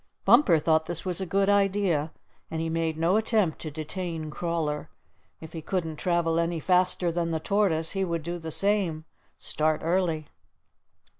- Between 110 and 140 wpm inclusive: No, average, 165 wpm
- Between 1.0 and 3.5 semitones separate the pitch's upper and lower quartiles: Yes, average, 2.7 semitones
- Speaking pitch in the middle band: Yes, medium, 170 Hz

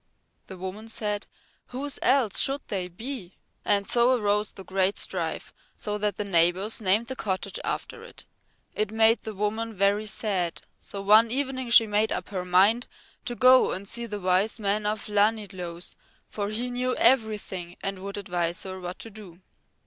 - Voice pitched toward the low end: No, high, 210 Hz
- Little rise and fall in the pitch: No, average, 3.1 semitones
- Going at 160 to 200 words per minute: Yes, average, 170 wpm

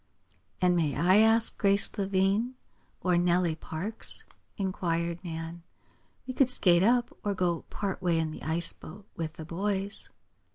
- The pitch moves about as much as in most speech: Yes, average, 3.1 semitones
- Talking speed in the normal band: Yes, average, 150 wpm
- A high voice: No, medium, 180 Hz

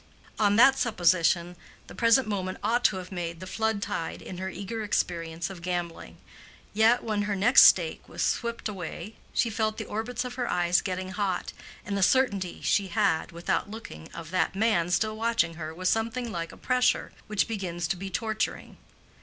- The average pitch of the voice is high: Yes, high, 200 Hz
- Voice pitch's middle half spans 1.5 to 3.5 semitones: No, average, 4.0 semitones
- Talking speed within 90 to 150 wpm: No, average, 185 wpm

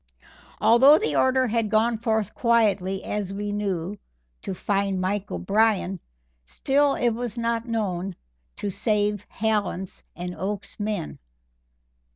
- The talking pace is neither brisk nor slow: No, slow, 130 wpm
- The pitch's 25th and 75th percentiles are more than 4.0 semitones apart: No, average, 2.9 semitones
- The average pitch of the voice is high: Yes, high, 210 Hz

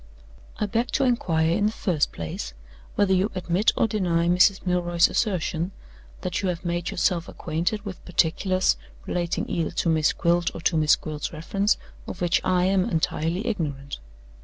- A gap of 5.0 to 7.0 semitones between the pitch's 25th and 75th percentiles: No, average, 2.8 semitones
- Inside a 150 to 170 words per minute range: Yes, average, 165 wpm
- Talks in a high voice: No, medium, 175 Hz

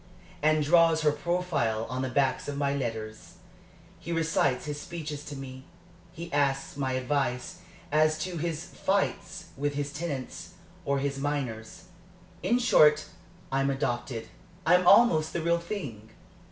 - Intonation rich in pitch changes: No, average, 3.8 semitones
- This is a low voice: No, medium, 145 Hz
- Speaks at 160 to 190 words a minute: No, average, 140 wpm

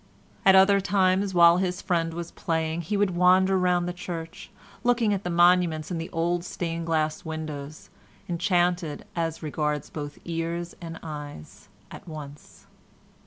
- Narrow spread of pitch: Yes, narrow, 2.1 semitones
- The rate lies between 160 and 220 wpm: No, average, 150 wpm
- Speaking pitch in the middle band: Yes, medium, 170 Hz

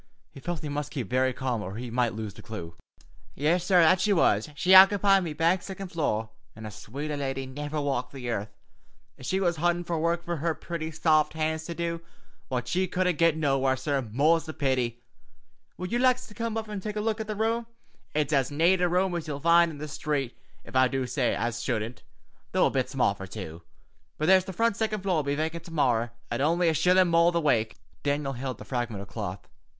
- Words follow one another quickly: Yes, fast, 230 wpm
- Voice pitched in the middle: Yes, medium, 155 Hz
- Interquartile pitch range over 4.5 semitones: Yes, average, 5.2 semitones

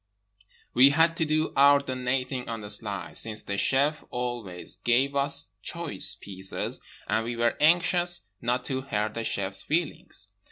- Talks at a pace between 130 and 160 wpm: Yes, average, 155 wpm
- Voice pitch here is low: Yes, low, 125 Hz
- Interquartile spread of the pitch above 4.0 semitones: Yes, average, 5.0 semitones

